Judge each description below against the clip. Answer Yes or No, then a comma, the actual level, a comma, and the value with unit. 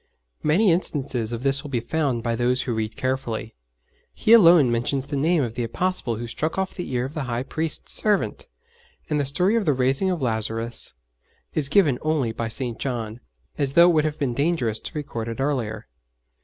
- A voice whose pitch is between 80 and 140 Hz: Yes, low, 135 Hz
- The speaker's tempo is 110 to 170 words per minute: No, average, 200 wpm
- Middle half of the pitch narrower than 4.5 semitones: No, average, 5.0 semitones